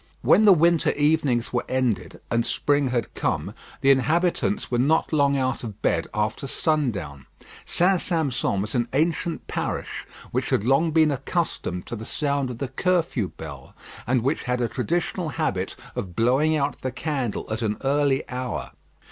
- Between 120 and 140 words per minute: No, average, 165 wpm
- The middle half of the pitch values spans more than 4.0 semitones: Yes, average, 4.8 semitones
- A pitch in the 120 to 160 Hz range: Yes, low, 135 Hz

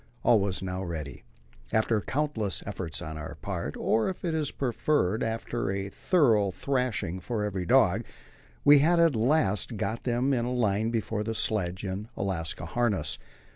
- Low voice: Yes, low, 110 Hz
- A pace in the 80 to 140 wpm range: No, average, 165 wpm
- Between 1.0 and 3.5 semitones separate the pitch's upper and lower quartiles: No, average, 4.8 semitones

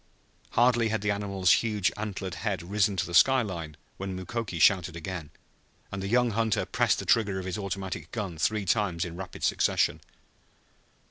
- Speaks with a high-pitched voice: No, very low, 95 Hz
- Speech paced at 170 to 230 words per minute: Yes, average, 175 wpm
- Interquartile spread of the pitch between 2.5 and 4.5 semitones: Yes, average, 3.0 semitones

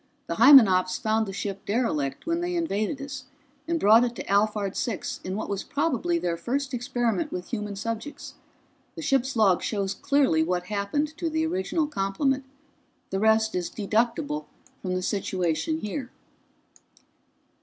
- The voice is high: Yes, high, 225 Hz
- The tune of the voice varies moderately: No, wide, 6.4 semitones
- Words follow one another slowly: No, average, 155 wpm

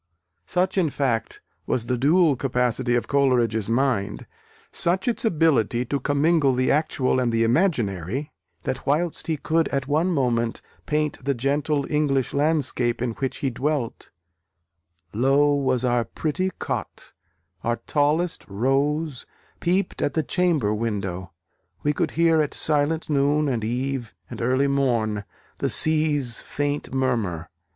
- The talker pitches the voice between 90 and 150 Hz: Yes, low, 135 Hz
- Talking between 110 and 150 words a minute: Yes, average, 140 wpm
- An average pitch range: Yes, average, 4.1 semitones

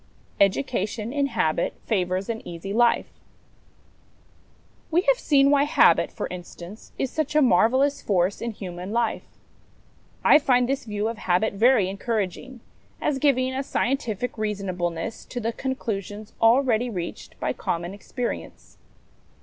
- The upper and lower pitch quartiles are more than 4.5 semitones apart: Yes, average, 5.1 semitones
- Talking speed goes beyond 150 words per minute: No, average, 140 wpm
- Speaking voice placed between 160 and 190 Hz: No, high, 225 Hz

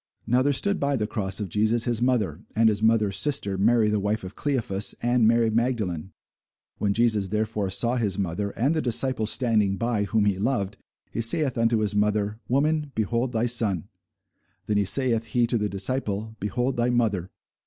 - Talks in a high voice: No, low, 110 Hz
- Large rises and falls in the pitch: No, average, 2.9 semitones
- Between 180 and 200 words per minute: Yes, average, 185 wpm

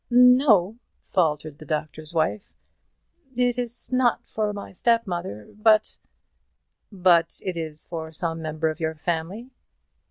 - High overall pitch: No, medium, 175 Hz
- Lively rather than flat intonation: Yes, wide, 5.8 semitones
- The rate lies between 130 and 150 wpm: Yes, slow, 135 wpm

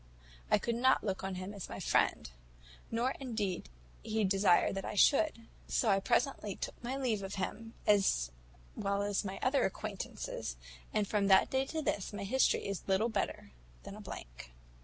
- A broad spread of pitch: No, average, 3.5 semitones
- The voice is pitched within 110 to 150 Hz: No, high, 205 Hz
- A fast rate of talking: No, average, 185 wpm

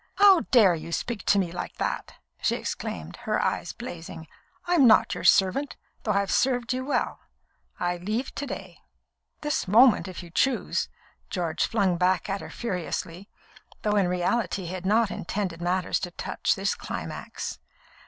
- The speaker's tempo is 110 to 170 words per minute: Yes, average, 165 wpm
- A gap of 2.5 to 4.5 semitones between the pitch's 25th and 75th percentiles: No, average, 5.0 semitones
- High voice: Yes, high, 195 Hz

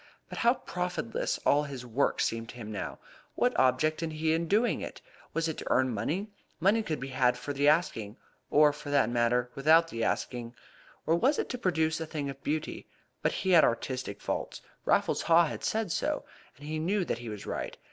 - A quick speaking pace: Yes, fast, 210 wpm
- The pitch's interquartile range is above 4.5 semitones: Yes, average, 5.1 semitones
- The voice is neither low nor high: Yes, medium, 150 Hz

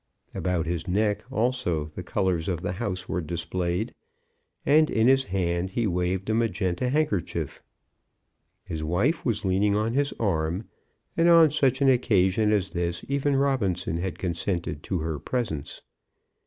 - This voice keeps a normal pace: Yes, average, 150 wpm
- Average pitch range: No, wide, 5.7 semitones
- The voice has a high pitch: No, very low, 95 Hz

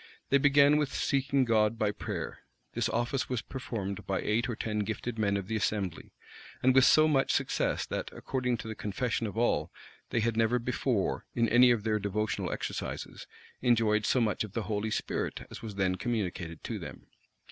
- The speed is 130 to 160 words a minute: No, average, 190 wpm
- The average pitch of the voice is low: Yes, low, 115 Hz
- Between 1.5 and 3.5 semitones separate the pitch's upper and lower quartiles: Yes, average, 3.0 semitones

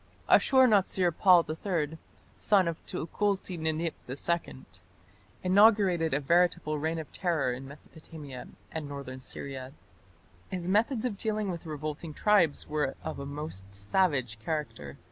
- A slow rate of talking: Yes, slow, 130 wpm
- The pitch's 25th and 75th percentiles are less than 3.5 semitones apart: No, average, 4.6 semitones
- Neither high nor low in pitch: Yes, medium, 160 Hz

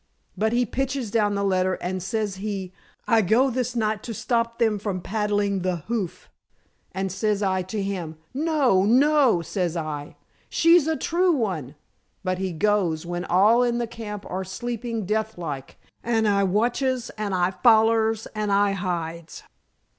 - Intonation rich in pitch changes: No, average, 3.8 semitones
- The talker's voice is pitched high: Yes, high, 210 Hz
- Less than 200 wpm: Yes, average, 160 wpm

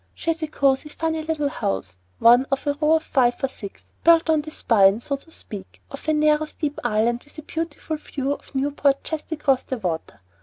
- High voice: Yes, very high, 285 Hz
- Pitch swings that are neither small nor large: Yes, average, 4.2 semitones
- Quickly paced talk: Yes, fast, 215 wpm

